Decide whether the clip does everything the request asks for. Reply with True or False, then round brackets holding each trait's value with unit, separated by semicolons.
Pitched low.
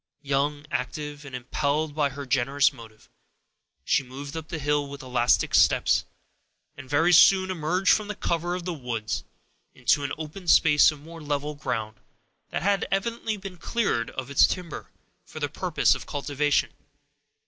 False (145 Hz)